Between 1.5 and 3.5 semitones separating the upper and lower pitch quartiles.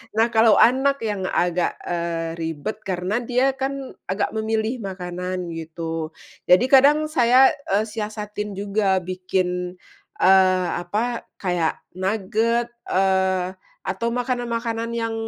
No: average, 3.9 semitones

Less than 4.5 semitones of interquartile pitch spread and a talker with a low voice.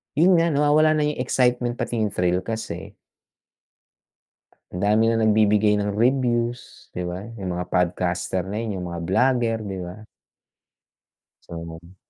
No: average, 5.2 semitones; low, 105 Hz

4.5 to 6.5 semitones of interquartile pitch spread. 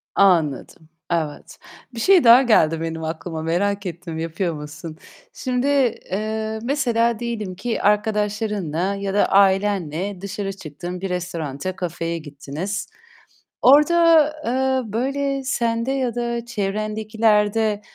Yes: wide, 5.5 semitones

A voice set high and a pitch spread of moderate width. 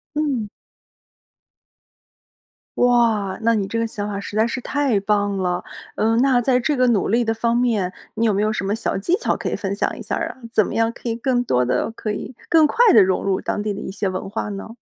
Yes: high, 220 Hz; average, 3.2 semitones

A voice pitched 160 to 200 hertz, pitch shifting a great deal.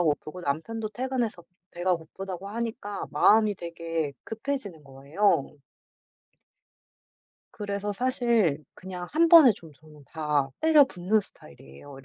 Yes: high, 190 Hz; wide, 6.1 semitones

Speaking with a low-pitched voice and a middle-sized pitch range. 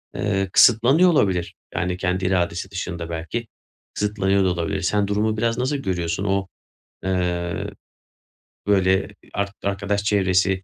No: very low, 95 Hz; narrow, 2.2 semitones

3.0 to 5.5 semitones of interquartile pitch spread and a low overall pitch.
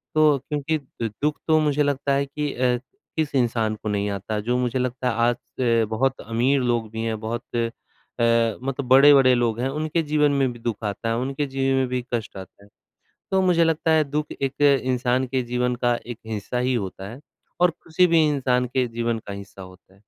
Yes: average, 3.7 semitones; low, 125 Hz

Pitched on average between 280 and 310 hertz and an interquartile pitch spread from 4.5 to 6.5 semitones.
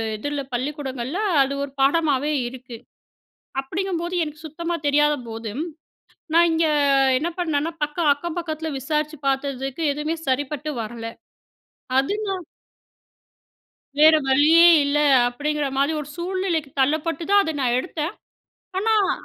No: very high, 300 Hz; average, 3.4 semitones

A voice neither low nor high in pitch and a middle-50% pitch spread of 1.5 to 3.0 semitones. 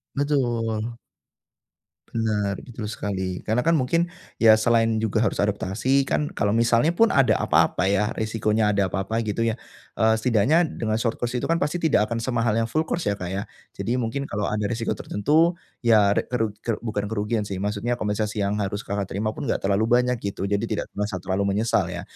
No: low, 110 Hz; average, 2.7 semitones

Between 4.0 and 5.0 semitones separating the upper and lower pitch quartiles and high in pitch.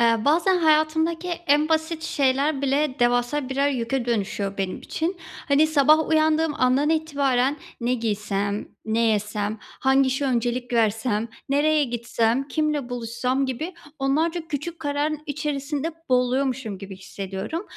Yes: average, 4.7 semitones; very high, 270 Hz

